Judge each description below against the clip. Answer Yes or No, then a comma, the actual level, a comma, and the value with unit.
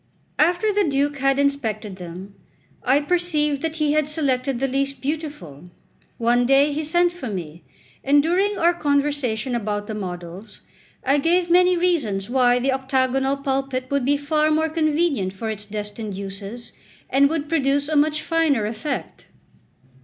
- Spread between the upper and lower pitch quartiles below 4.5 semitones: No, wide, 5.4 semitones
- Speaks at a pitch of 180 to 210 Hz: No, very high, 275 Hz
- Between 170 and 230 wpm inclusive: No, average, 155 wpm